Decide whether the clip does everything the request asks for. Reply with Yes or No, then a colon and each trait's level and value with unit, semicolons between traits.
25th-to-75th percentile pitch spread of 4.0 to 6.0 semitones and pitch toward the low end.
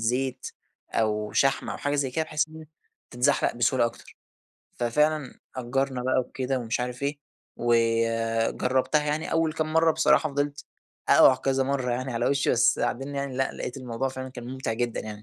No: average, 3.0 semitones; low, 130 Hz